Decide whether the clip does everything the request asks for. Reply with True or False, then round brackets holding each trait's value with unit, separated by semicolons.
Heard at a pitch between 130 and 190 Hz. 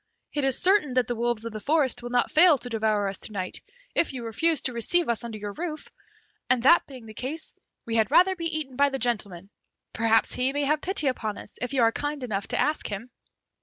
False (250 Hz)